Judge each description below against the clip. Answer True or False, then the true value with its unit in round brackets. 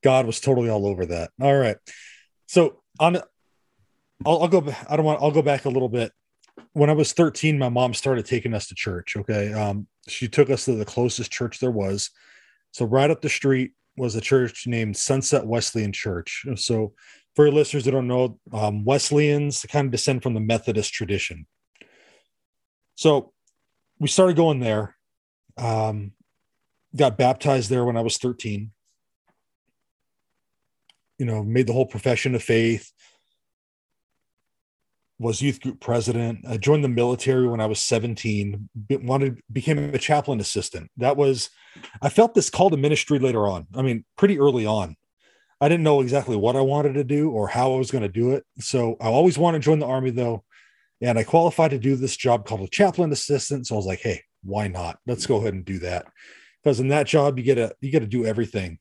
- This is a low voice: True (125 Hz)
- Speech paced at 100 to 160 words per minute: False (190 wpm)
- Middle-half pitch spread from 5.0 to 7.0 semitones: False (4.4 semitones)